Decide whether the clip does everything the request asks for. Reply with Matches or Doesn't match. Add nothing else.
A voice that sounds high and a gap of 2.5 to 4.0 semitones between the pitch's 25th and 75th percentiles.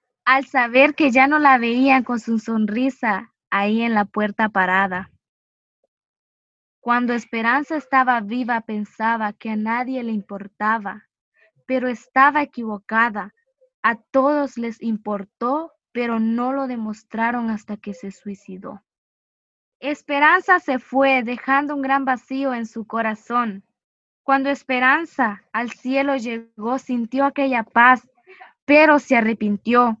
Matches